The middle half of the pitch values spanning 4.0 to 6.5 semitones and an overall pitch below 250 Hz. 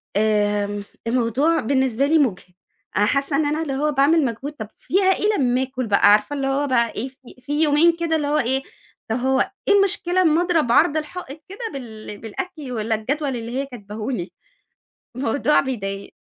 No: average, 5.1 semitones; very high, 265 Hz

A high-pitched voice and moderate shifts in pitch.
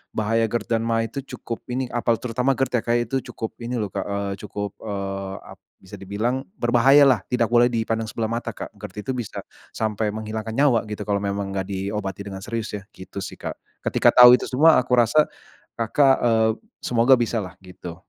No: low, 115 Hz; average, 3.1 semitones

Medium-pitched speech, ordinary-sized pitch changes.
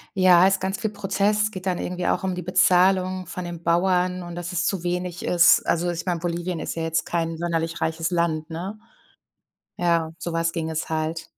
No: medium, 175 Hz; narrow, 1.7 semitones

